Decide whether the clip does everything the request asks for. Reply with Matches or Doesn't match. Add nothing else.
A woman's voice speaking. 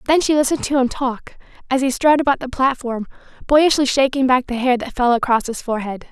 Matches